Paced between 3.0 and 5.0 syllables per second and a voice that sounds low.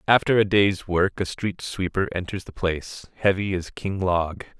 Yes: 4.5 syllables/s; very low, 95 Hz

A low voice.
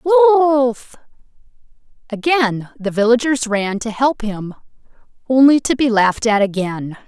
No: high, 240 Hz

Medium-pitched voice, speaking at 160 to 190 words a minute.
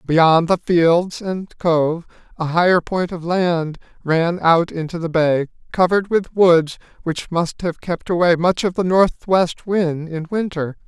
Yes: medium, 170 Hz; average, 165 wpm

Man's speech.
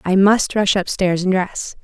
No: female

